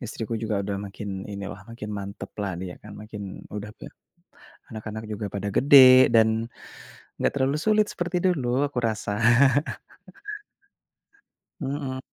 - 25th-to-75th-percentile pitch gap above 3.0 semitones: Yes, average, 4.3 semitones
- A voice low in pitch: Yes, low, 110 Hz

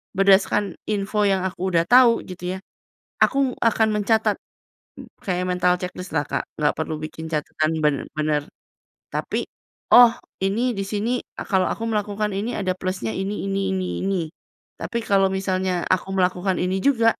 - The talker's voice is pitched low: No, high, 190 Hz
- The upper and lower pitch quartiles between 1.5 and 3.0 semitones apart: Yes, narrow, 2.6 semitones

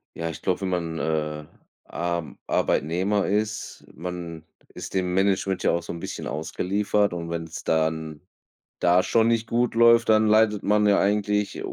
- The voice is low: Yes, very low, 95 Hz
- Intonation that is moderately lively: Yes, average, 4.0 semitones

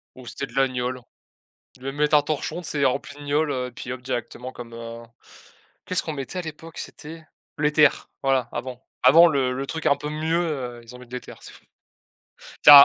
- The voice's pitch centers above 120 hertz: Yes, medium, 140 Hz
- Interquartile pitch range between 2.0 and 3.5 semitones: Yes, average, 3.2 semitones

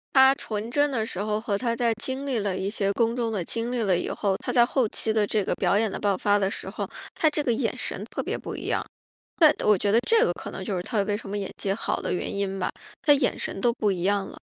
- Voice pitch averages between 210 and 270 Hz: Yes, high, 215 Hz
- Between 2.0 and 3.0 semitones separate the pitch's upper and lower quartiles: No, average, 3.4 semitones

